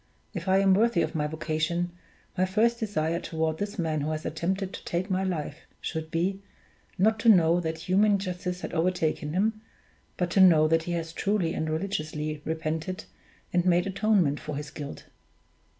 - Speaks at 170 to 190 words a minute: Yes, average, 180 wpm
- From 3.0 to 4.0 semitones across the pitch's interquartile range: Yes, average, 3.3 semitones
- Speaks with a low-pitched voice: No, medium, 175 Hz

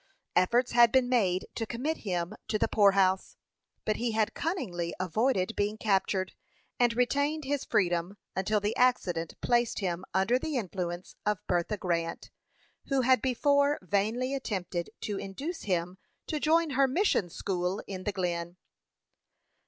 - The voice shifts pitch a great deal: Yes, wide, 5.7 semitones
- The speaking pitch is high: Yes, high, 210 Hz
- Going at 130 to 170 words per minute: Yes, average, 145 wpm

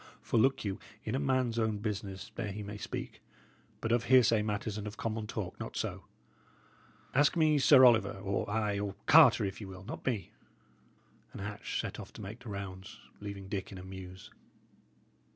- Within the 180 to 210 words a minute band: Yes, average, 185 wpm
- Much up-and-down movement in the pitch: No, average, 3.0 semitones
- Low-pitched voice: Yes, low, 105 Hz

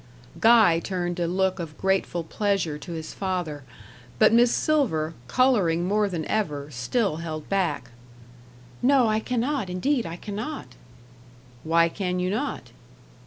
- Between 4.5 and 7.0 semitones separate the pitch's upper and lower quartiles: Yes, average, 4.9 semitones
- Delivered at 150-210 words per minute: No, slow, 135 wpm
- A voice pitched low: No, medium, 185 Hz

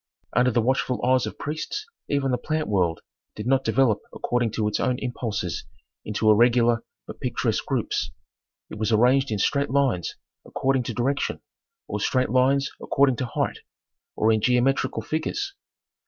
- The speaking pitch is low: Yes, low, 125 Hz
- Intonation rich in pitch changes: No, average, 3.3 semitones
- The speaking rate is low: No, average, 155 wpm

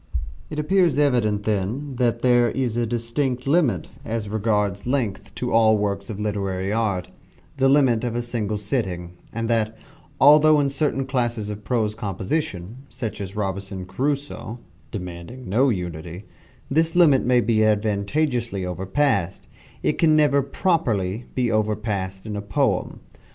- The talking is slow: No, average, 145 wpm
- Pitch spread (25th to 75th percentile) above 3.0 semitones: Yes, average, 4.7 semitones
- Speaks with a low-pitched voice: Yes, low, 115 Hz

